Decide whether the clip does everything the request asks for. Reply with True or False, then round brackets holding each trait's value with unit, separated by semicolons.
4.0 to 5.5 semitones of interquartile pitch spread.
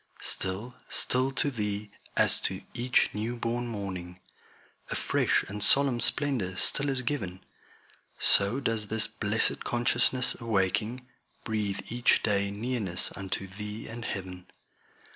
False (3.4 semitones)